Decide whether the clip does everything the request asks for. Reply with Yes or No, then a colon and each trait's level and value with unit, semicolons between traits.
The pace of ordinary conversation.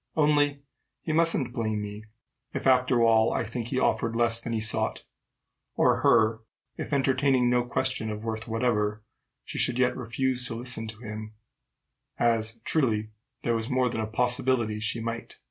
Yes: average, 170 wpm